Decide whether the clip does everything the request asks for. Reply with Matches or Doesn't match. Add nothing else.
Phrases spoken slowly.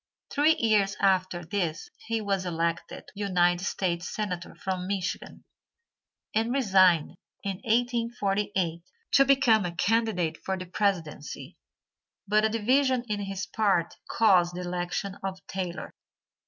Matches